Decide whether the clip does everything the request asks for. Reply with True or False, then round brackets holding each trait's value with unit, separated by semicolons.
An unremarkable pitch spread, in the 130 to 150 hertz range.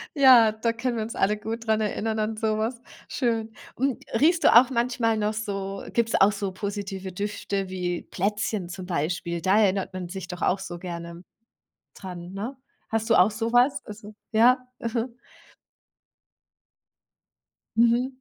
False (3.3 semitones; 215 Hz)